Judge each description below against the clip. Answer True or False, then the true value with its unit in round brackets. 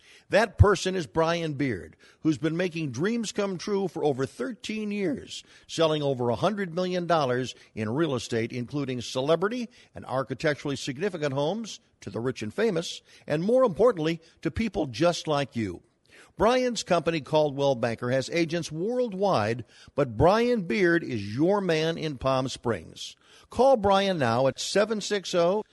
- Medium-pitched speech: True (160 Hz)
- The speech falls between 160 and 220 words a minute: False (145 wpm)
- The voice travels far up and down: True (6.7 semitones)